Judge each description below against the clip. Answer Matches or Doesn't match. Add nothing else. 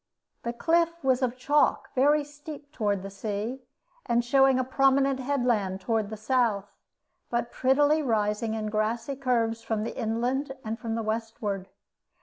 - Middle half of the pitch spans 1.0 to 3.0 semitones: Doesn't match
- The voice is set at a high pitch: Matches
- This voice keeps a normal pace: Matches